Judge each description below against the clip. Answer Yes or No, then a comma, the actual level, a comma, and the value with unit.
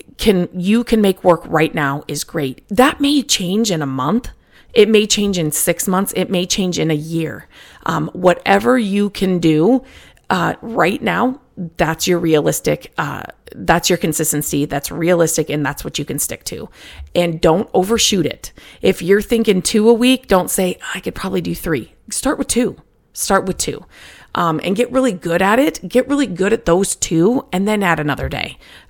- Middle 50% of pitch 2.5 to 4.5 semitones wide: No, average, 5.3 semitones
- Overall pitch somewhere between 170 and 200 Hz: Yes, medium, 185 Hz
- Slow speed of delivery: No, average, 190 wpm